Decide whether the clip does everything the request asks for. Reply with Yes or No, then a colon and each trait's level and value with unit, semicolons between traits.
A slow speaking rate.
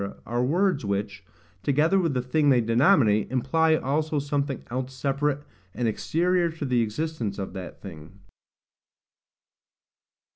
Yes: slow, 125 wpm